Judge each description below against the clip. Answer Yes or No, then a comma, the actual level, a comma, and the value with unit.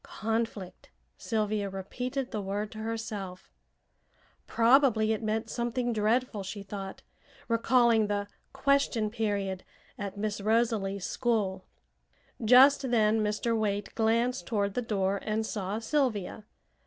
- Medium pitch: No, high, 215 Hz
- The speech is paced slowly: Yes, slow, 115 wpm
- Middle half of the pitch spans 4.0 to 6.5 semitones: No, narrow, 2.5 semitones